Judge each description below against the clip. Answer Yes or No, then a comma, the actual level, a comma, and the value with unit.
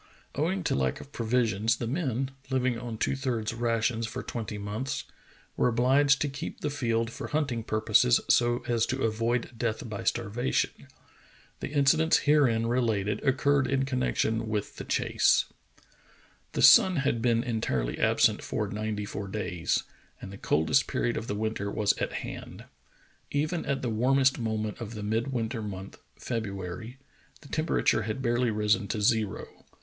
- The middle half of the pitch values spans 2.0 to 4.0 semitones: Yes, average, 3.5 semitones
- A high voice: No, low, 115 Hz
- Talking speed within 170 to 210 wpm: No, average, 155 wpm